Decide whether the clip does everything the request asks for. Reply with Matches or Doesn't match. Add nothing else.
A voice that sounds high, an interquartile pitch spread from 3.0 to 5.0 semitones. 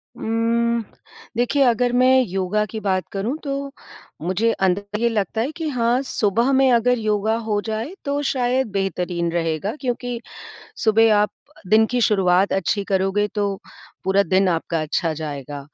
Matches